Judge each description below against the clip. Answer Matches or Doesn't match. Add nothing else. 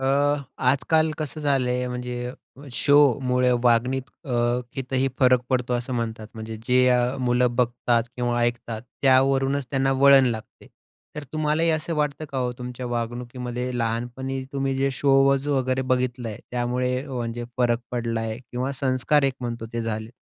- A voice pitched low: Matches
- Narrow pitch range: Matches